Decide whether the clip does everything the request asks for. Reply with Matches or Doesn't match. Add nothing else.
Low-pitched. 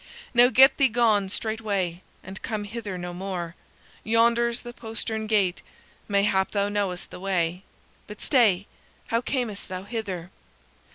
Doesn't match